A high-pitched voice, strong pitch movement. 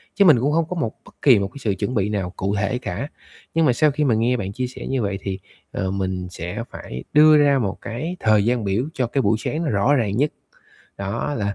No: low, 115 Hz; wide, 6.0 semitones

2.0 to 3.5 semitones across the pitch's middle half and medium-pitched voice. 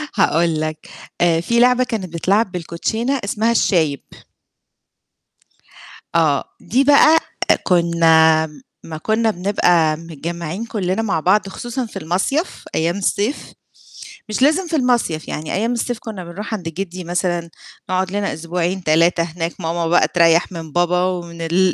No: average, 4.6 semitones; medium, 180 Hz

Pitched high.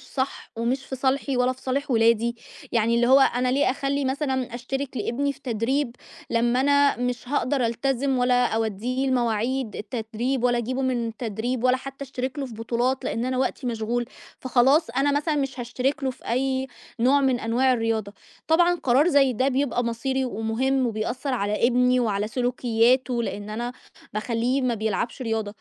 Yes: very high, 250 Hz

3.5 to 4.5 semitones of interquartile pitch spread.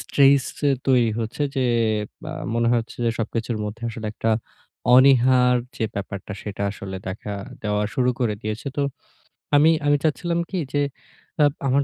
Yes: average, 4.1 semitones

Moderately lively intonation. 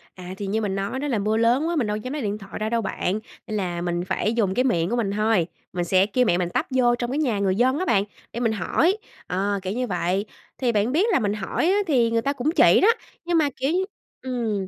Yes: average, 4.6 semitones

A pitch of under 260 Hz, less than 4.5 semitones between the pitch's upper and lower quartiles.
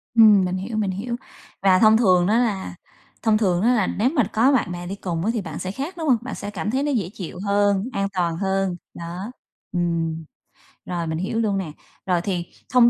Yes: high, 195 Hz; average, 4.0 semitones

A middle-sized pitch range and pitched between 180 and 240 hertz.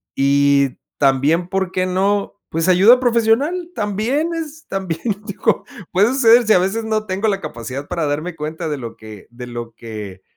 No: wide, 7.7 semitones; medium, 185 Hz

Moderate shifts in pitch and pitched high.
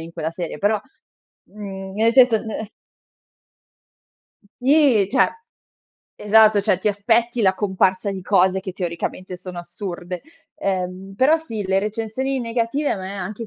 Yes: average, 3.3 semitones; high, 200 Hz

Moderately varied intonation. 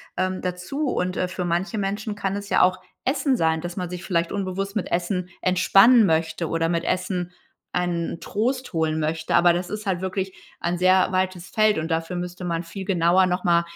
No: narrow, 2.2 semitones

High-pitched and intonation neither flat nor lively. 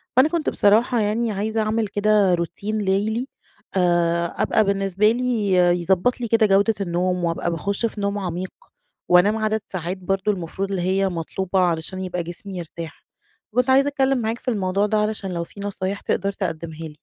Yes: high, 195 Hz; average, 3.3 semitones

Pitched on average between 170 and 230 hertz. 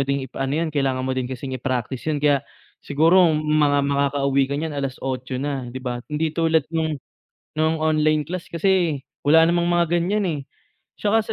No: medium, 145 Hz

